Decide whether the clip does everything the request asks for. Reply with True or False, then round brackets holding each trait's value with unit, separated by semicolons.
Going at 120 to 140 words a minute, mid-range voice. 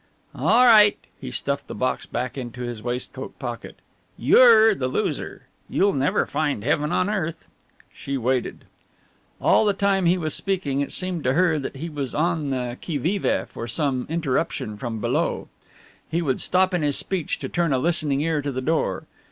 False (180 wpm; 150 Hz)